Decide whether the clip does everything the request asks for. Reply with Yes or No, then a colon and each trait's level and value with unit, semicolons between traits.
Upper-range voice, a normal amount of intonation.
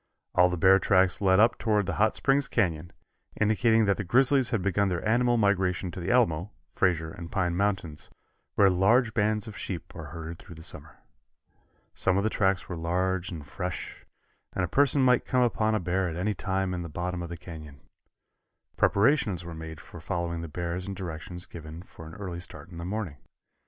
No: very low, 95 Hz; average, 3.5 semitones